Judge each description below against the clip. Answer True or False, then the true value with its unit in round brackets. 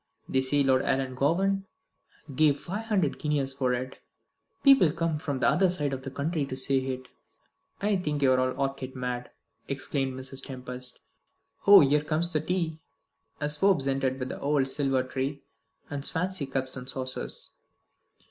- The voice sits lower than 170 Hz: True (140 Hz)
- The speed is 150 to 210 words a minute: True (165 wpm)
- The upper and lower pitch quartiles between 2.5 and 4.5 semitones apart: True (3.1 semitones)